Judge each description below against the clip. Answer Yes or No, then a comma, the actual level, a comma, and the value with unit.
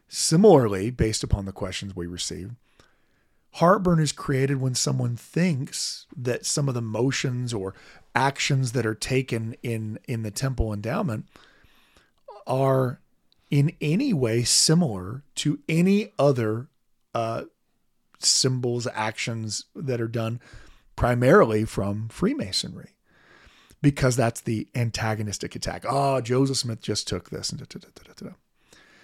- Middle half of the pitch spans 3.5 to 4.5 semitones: Yes, average, 3.8 semitones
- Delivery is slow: Yes, slow, 130 wpm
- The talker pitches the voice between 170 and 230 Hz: No, low, 125 Hz